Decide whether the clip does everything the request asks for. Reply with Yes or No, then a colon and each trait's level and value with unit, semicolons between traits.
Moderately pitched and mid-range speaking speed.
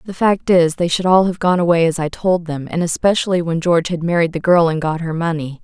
No: medium, 170 Hz; fast, 265 wpm